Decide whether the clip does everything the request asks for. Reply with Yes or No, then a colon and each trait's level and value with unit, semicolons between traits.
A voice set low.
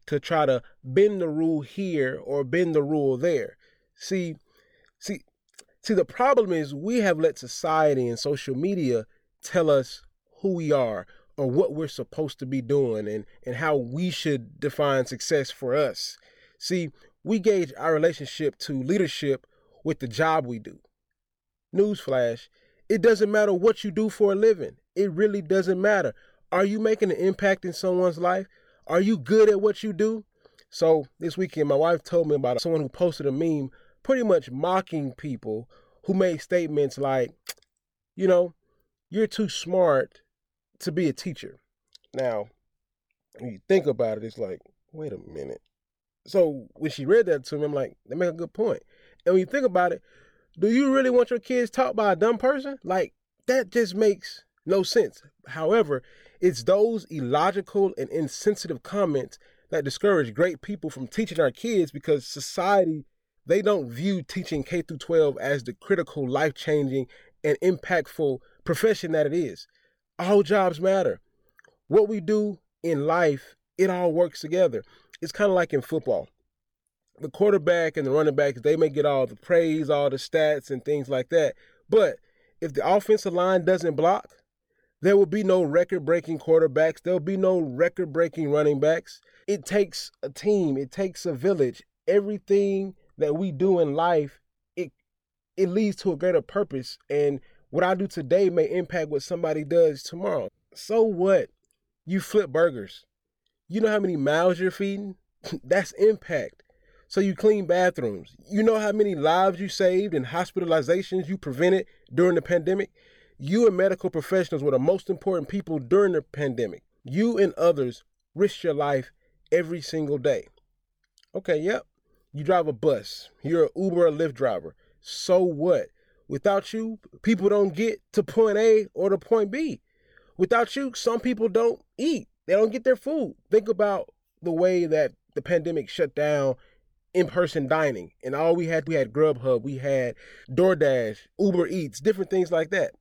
No: medium, 180 Hz